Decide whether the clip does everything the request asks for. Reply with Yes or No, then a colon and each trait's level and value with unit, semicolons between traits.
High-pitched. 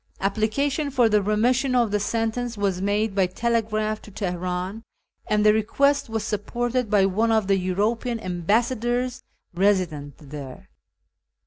Yes: high, 215 Hz